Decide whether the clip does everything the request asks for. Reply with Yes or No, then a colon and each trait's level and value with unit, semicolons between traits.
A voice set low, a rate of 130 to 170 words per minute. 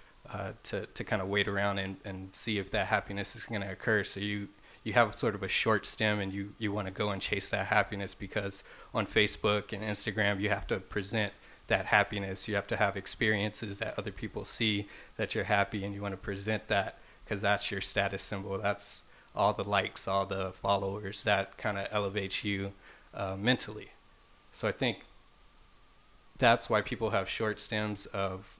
No: low, 100 Hz; average, 200 wpm